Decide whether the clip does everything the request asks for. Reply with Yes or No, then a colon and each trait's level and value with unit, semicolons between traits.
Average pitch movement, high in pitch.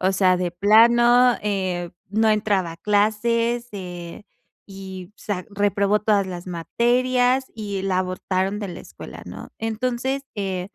Yes: average, 3.8 semitones; high, 205 Hz